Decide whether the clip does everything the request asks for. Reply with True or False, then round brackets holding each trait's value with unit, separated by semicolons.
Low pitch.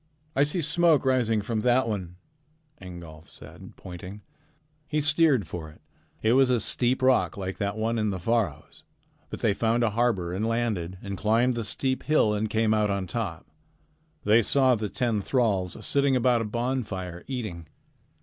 True (110 Hz)